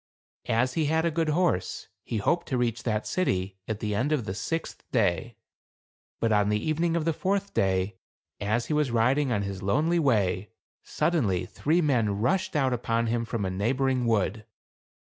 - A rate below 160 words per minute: No, average, 185 wpm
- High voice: No, low, 120 Hz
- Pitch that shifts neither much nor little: No, wide, 6.6 semitones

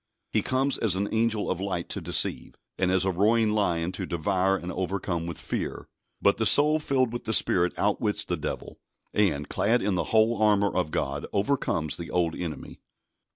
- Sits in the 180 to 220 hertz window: No, low, 100 Hz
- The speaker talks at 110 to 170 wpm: No, average, 190 wpm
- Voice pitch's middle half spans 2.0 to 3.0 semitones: No, average, 3.9 semitones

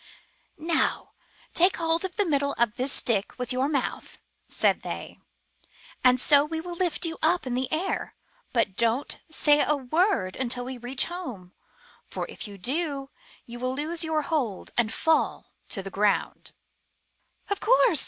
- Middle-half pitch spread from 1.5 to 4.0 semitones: No, average, 5.1 semitones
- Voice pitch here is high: Yes, very high, 280 Hz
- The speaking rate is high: No, average, 165 wpm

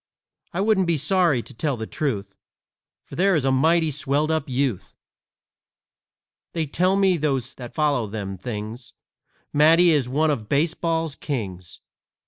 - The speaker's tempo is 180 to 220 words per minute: No, average, 145 wpm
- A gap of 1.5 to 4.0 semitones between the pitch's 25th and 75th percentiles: No, average, 5.2 semitones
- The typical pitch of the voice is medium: Yes, medium, 145 Hz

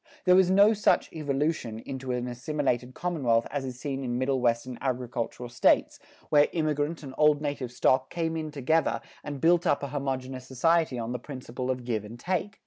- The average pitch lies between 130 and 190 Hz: Yes, low, 135 Hz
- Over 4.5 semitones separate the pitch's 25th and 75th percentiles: No, average, 3.8 semitones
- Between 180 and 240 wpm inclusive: Yes, average, 185 wpm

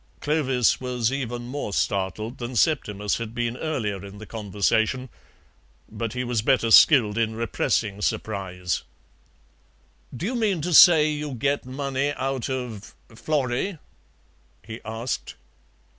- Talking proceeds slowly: Yes, slow, 130 wpm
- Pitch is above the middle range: No, low, 120 Hz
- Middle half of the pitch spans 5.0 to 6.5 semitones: No, average, 4.0 semitones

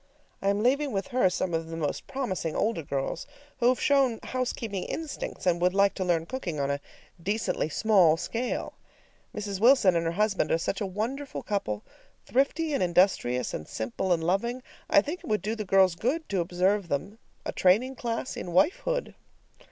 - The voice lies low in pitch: No, high, 200 Hz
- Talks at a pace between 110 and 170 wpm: No, average, 185 wpm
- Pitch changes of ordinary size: No, wide, 5.9 semitones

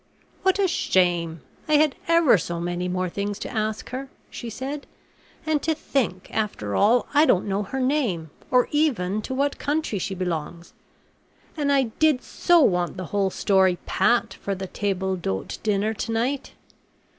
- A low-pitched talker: No, high, 215 Hz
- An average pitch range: No, wide, 7.2 semitones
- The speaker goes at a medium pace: Yes, average, 170 wpm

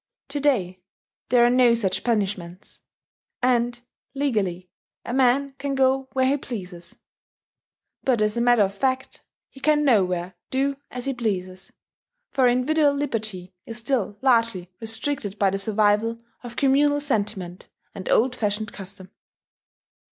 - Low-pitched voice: No, high, 235 Hz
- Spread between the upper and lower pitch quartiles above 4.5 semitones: Yes, average, 5.1 semitones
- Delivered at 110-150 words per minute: Yes, slow, 135 wpm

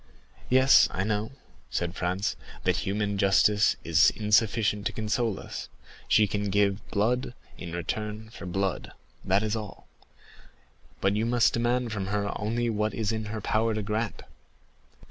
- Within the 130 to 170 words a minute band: Yes, average, 155 wpm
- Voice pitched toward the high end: No, low, 105 Hz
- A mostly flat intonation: Yes, narrow, 2.0 semitones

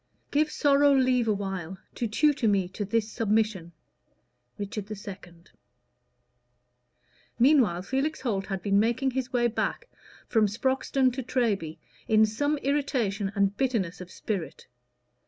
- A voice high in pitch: Yes, high, 225 Hz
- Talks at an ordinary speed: No, slow, 125 wpm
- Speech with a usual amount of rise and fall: Yes, average, 4.9 semitones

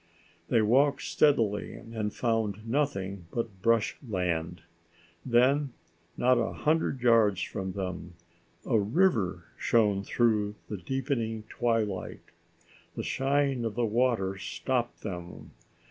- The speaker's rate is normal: No, slow, 115 wpm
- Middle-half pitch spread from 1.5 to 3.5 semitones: No, average, 4.2 semitones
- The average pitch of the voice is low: Yes, low, 115 Hz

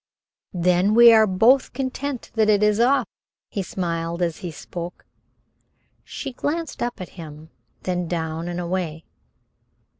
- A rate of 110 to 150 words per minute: Yes, average, 140 wpm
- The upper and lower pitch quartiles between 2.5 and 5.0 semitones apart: No, wide, 5.4 semitones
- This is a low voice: No, medium, 185 Hz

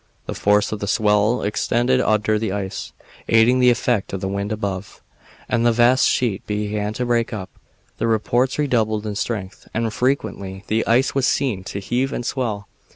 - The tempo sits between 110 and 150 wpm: No, average, 180 wpm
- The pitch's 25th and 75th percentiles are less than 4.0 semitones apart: Yes, average, 2.9 semitones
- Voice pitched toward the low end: Yes, low, 110 Hz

